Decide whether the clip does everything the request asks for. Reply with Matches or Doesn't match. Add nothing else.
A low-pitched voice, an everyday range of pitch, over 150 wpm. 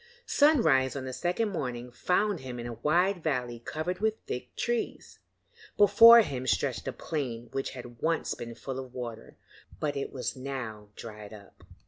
Doesn't match